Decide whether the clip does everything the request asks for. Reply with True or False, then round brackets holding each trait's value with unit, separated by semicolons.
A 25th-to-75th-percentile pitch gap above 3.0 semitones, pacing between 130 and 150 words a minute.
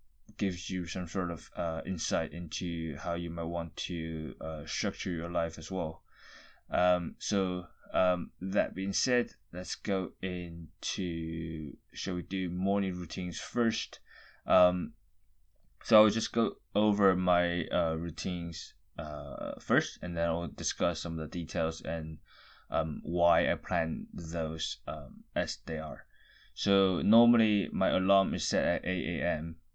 False (2.4 semitones; 145 wpm)